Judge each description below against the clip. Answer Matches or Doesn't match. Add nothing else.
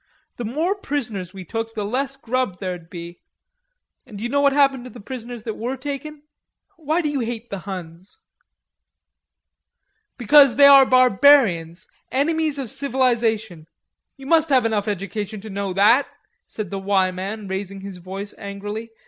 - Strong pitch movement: Matches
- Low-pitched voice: Doesn't match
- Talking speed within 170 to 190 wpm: Doesn't match